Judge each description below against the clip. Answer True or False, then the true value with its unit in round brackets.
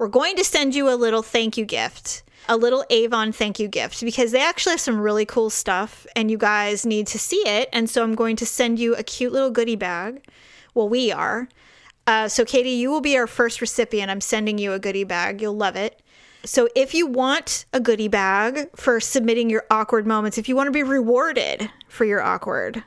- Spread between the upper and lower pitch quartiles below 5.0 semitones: True (2.8 semitones)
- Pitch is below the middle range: False (235 Hz)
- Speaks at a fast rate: True (225 wpm)